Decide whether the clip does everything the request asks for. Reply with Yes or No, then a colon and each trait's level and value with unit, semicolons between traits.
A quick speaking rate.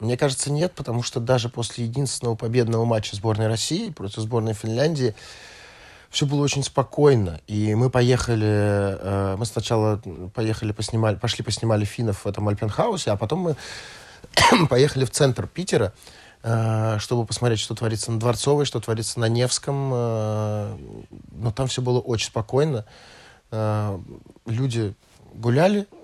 No: average, 140 wpm